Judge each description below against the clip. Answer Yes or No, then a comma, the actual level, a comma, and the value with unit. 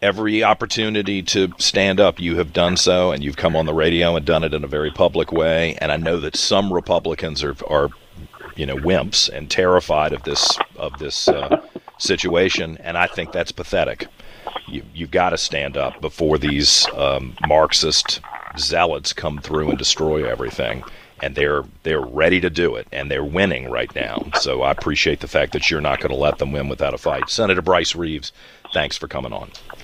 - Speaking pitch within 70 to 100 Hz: Yes, very low, 80 Hz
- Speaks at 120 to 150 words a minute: No, average, 195 wpm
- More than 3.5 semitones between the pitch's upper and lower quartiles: No, average, 2.8 semitones